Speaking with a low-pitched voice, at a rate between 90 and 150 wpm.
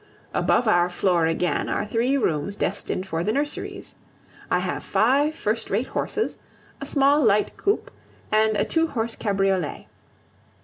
No: high, 215 Hz; average, 145 wpm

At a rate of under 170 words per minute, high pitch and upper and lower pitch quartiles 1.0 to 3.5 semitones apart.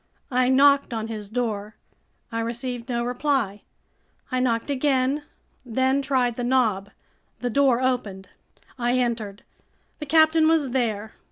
Yes: slow, 135 wpm; high, 245 Hz; average, 2.8 semitones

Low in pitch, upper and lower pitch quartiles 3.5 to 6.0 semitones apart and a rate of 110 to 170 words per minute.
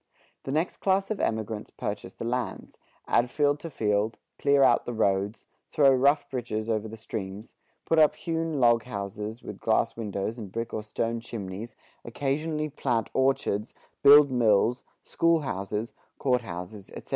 Yes: low, 115 Hz; average, 4.9 semitones; average, 155 wpm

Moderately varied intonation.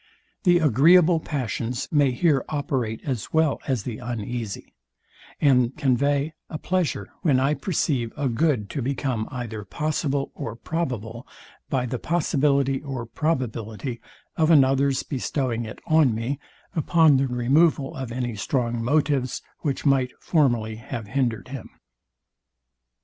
Yes: average, 3.9 semitones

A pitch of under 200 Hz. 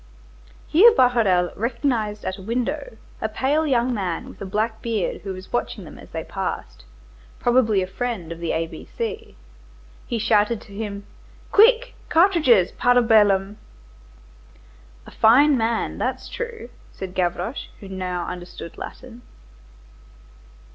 No: high, 225 Hz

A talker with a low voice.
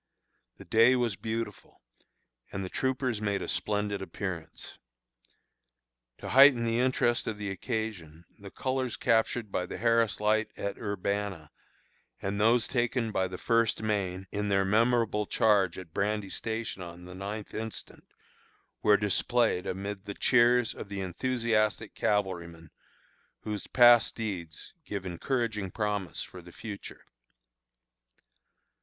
Yes: low, 105 Hz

